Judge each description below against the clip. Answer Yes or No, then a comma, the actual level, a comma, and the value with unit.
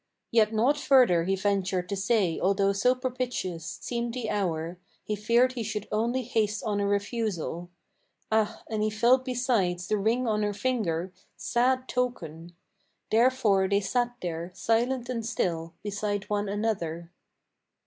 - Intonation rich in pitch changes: No, average, 4.0 semitones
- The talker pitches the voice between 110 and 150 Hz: No, high, 210 Hz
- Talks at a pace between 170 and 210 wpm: No, average, 150 wpm